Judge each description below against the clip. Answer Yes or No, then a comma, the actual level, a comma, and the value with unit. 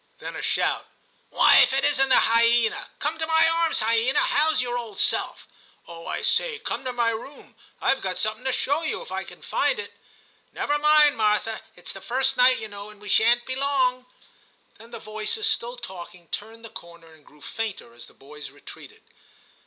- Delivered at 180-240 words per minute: Yes, average, 200 wpm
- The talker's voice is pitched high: Yes, high, 235 Hz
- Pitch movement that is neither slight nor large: Yes, average, 4.7 semitones